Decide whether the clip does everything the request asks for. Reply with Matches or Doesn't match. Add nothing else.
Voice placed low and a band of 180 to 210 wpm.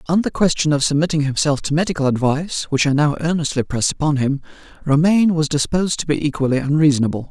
Doesn't match